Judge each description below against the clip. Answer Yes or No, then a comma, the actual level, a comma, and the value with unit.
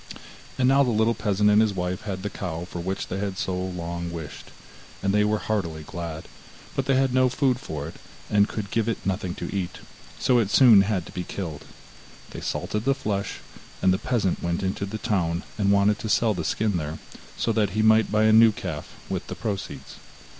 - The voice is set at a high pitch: No, low, 100 Hz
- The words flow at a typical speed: No, fast, 215 wpm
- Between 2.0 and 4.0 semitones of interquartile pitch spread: Yes, average, 3.5 semitones